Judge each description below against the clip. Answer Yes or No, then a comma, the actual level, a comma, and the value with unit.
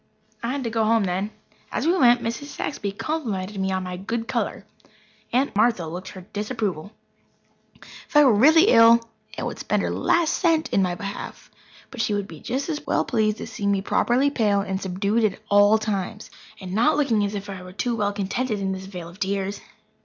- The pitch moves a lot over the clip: No, average, 3.8 semitones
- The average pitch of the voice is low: No, high, 210 Hz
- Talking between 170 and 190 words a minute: No, fast, 205 wpm